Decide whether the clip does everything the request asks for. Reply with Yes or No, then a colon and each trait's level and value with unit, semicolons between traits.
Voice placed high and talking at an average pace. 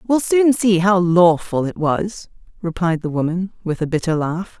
No: medium, 180 Hz; average, 185 wpm